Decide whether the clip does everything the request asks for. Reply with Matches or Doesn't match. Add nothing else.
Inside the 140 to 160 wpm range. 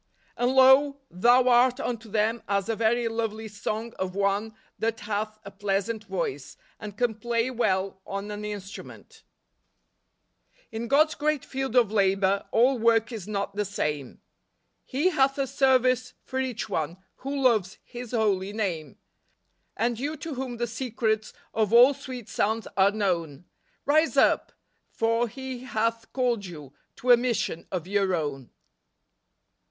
Matches